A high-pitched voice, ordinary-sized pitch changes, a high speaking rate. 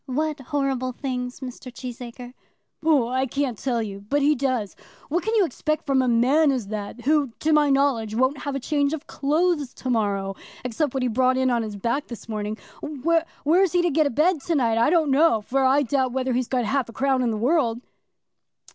Yes: very high, 265 Hz; average, 3.6 semitones; fast, 220 wpm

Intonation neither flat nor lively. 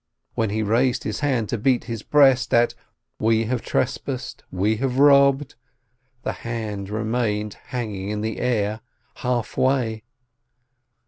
Yes: average, 3.0 semitones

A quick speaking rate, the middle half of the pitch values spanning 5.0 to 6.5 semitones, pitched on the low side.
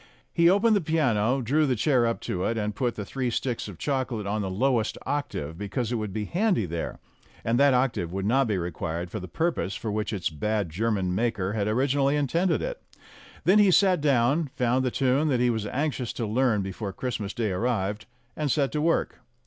Yes: fast, 210 wpm; average, 5.3 semitones; low, 120 Hz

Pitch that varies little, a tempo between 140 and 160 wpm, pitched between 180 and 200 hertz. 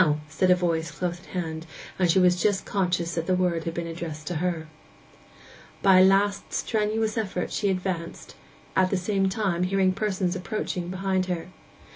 No: narrow, 2.2 semitones; average, 175 wpm; medium, 185 Hz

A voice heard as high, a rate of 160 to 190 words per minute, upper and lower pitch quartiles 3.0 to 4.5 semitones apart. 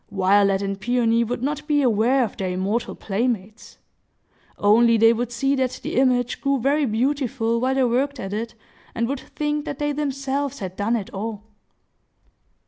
Yes: high, 240 Hz; average, 165 wpm; average, 4.2 semitones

